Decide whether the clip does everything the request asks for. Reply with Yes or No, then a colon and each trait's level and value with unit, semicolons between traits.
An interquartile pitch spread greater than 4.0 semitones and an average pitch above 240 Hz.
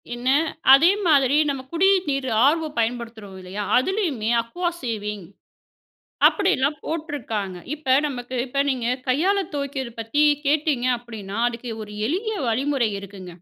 Yes: average, 4.7 semitones; very high, 260 Hz